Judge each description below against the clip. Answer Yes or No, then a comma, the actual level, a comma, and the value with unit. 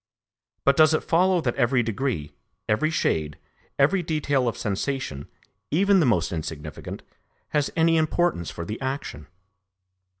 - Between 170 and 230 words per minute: No, slow, 135 wpm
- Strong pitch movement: Yes, wide, 8.5 semitones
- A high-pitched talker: No, low, 135 Hz